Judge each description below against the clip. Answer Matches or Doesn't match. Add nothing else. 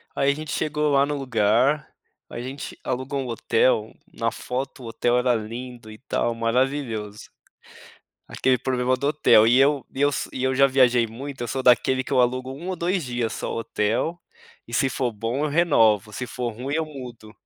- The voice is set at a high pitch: Doesn't match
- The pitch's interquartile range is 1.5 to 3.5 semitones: Matches